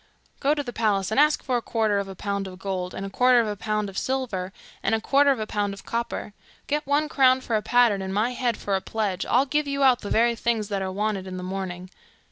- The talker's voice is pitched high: Yes, high, 215 Hz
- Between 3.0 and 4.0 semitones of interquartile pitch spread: No, average, 4.5 semitones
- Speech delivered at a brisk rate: Yes, fast, 265 wpm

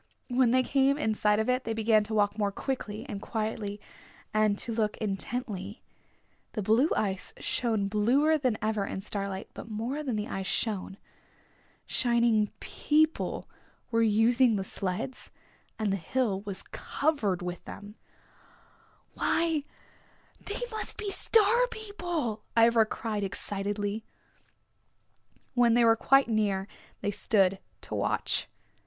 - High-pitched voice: Yes, high, 220 Hz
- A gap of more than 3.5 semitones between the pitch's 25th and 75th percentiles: Yes, average, 3.9 semitones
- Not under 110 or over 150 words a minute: Yes, slow, 135 wpm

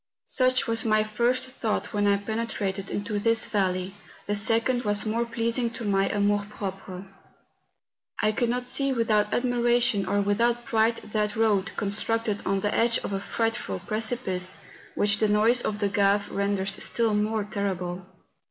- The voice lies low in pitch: No, high, 215 Hz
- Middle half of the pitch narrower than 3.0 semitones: Yes, narrow, 2.4 semitones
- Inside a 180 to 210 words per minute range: No, average, 160 wpm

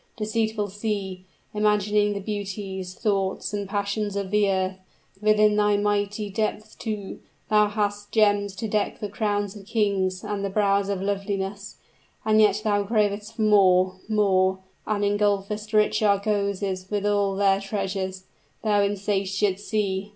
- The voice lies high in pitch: Yes, high, 205 Hz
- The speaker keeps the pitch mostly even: Yes, narrow, 1.3 semitones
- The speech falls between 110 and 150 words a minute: Yes, average, 145 wpm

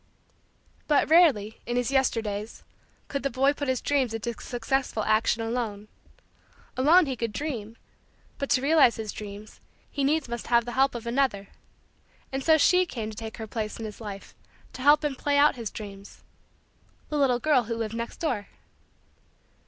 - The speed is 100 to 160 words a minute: No, average, 175 wpm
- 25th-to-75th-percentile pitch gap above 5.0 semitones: No, average, 4.2 semitones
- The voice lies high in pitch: Yes, high, 240 Hz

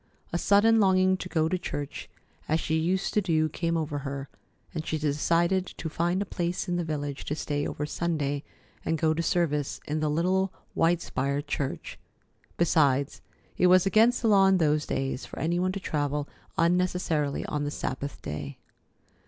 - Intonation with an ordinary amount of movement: Yes, average, 3.7 semitones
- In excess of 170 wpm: Yes, average, 180 wpm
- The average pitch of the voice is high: No, medium, 160 Hz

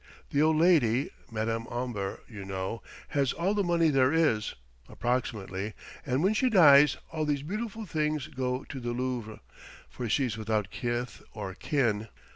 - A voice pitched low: Yes, low, 130 Hz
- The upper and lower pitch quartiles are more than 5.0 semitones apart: Yes, wide, 5.5 semitones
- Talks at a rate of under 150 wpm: No, average, 155 wpm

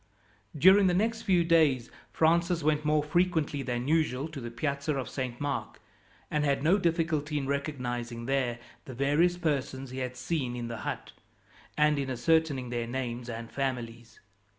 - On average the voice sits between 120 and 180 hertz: Yes, medium, 140 Hz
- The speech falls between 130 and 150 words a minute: No, average, 165 wpm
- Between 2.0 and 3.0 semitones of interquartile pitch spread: No, average, 4.2 semitones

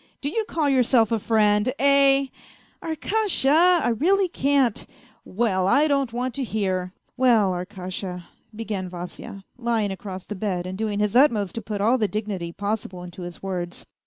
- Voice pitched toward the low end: No, high, 220 Hz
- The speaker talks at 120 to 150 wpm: No, average, 190 wpm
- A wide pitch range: Yes, wide, 6.0 semitones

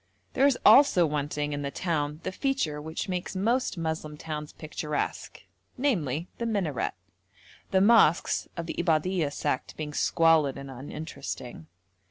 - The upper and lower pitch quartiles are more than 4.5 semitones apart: No, average, 4.1 semitones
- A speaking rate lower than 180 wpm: Yes, average, 140 wpm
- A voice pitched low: No, medium, 160 Hz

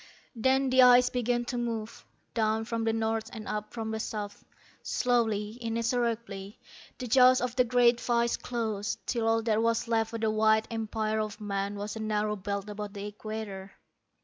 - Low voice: No, high, 225 Hz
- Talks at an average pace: Yes, average, 180 wpm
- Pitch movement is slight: Yes, narrow, 2.0 semitones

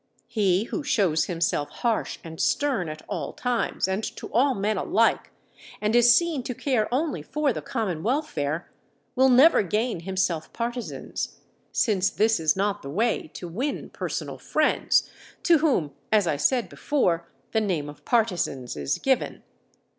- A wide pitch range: Yes, wide, 6.6 semitones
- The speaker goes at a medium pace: Yes, average, 155 wpm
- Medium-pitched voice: No, high, 215 Hz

